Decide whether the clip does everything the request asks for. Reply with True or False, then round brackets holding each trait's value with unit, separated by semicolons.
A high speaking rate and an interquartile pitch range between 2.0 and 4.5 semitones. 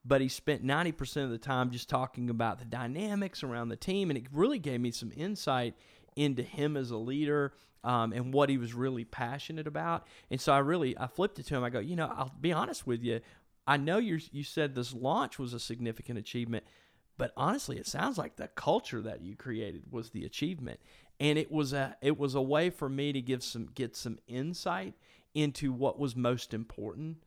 True (215 wpm; 3.6 semitones)